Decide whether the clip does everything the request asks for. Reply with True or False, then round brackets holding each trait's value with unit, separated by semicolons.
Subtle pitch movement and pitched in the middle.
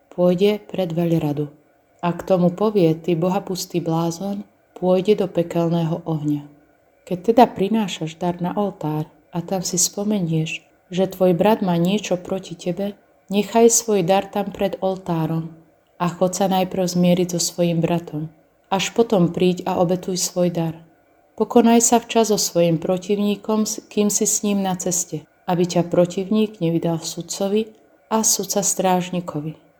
False (3.1 semitones; 180 Hz)